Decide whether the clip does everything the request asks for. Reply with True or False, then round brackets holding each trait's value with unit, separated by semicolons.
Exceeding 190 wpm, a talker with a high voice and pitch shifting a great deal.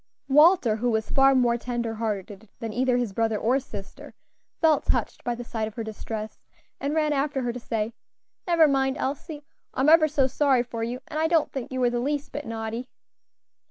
False (205 wpm; 250 Hz; 3.8 semitones)